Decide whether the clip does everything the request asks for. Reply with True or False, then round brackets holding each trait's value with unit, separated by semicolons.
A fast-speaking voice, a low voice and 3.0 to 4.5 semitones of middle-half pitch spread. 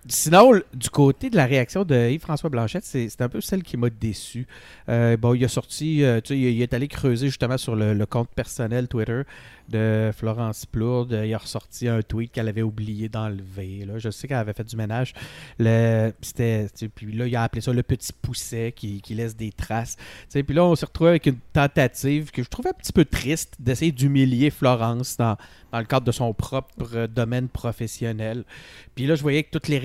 True (225 wpm; 120 Hz; 3.5 semitones)